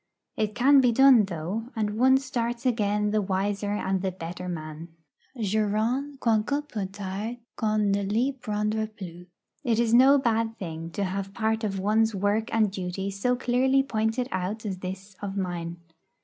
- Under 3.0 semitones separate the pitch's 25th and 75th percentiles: No, average, 3.5 semitones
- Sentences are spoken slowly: No, average, 165 wpm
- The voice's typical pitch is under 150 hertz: No, high, 210 Hz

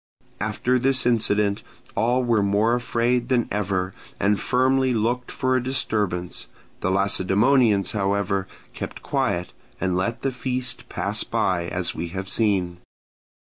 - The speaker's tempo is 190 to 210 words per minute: No, slow, 135 wpm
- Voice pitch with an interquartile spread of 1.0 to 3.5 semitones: No, average, 4.5 semitones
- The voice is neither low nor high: No, low, 105 Hz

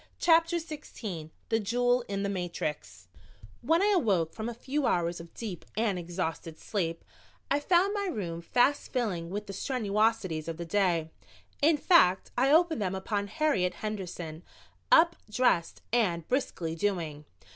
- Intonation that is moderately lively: No, wide, 7.4 semitones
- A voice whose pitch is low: No, high, 205 Hz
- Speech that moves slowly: No, average, 150 wpm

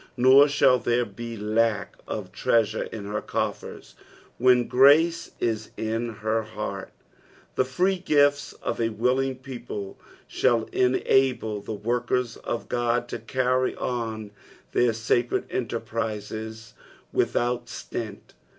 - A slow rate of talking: Yes, slow, 120 wpm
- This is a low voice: Yes, low, 120 Hz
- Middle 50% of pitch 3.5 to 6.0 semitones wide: No, narrow, 2.5 semitones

